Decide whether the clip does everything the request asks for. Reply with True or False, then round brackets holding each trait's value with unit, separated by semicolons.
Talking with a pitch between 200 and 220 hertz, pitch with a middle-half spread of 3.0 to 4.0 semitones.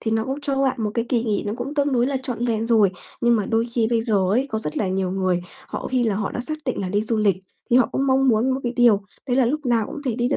False (235 Hz; 3.4 semitones)